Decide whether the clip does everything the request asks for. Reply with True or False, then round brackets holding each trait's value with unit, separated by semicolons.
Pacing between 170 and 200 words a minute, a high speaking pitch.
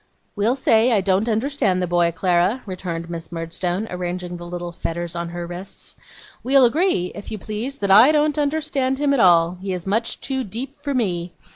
True (190 wpm; 195 Hz)